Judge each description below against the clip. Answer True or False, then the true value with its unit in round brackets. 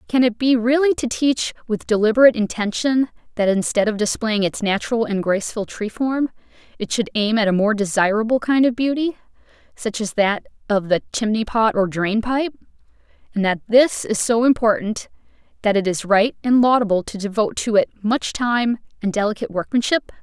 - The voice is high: True (225 Hz)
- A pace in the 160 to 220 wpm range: True (180 wpm)